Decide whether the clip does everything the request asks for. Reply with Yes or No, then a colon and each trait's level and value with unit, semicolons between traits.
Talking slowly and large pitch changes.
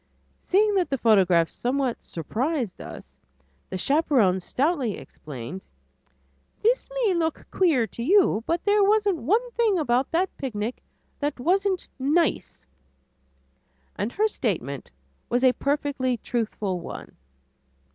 Yes: slow, 120 wpm; wide, 8.4 semitones